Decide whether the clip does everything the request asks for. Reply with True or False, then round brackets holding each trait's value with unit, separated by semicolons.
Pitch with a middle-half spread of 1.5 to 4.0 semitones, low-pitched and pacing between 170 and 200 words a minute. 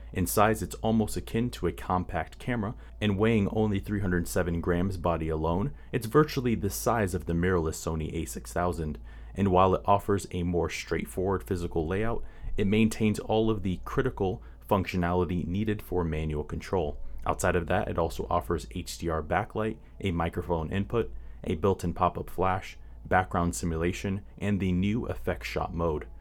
False (3.4 semitones; 90 Hz; 160 wpm)